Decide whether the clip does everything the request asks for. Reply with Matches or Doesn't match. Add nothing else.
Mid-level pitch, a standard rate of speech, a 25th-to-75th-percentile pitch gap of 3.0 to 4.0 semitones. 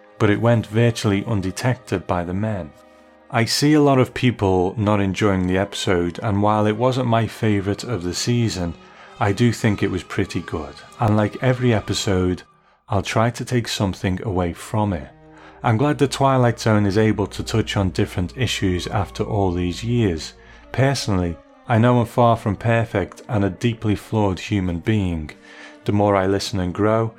Doesn't match